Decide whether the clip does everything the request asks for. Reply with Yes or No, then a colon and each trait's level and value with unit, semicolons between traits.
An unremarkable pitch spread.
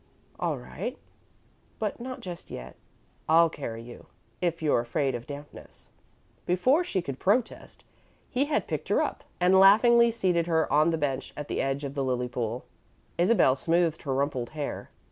No: wide, 5.8 semitones